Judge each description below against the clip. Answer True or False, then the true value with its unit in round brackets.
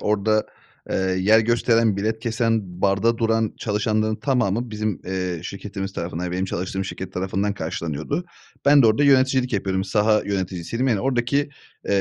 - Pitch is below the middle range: True (105 Hz)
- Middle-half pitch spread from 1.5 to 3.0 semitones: False (3.4 semitones)